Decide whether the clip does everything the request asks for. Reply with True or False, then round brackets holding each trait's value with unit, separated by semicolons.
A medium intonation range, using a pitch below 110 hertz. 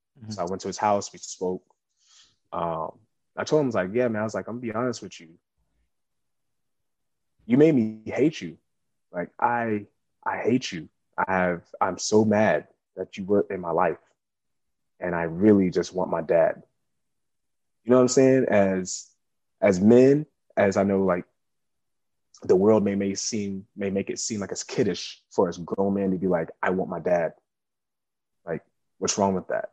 True (3.2 semitones; 100 Hz)